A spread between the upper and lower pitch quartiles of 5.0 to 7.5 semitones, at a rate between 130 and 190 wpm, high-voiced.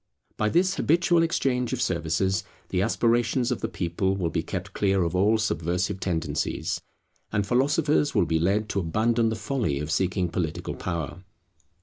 No: wide, 5.6 semitones; average, 160 wpm; very low, 95 Hz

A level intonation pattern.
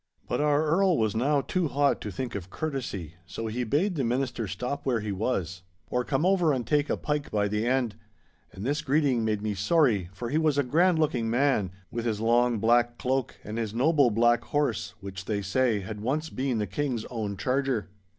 No: average, 5.0 semitones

